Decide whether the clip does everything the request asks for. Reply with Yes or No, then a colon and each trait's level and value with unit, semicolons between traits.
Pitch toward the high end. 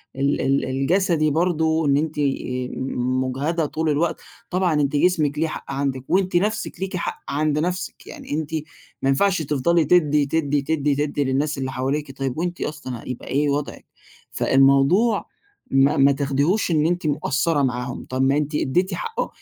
No: medium, 145 Hz